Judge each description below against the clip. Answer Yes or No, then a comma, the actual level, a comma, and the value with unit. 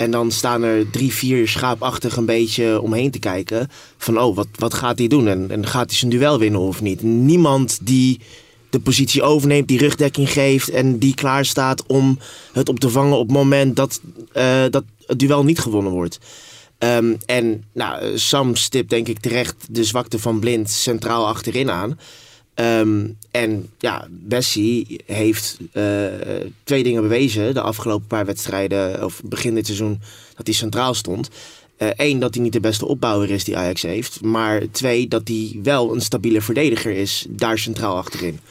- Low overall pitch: Yes, low, 115 Hz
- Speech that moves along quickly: No, average, 180 wpm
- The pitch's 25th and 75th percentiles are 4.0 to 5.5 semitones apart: No, average, 3.2 semitones